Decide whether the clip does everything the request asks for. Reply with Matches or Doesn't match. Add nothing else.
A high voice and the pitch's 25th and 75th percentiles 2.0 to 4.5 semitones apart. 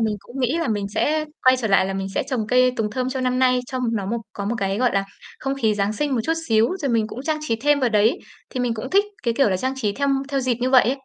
Matches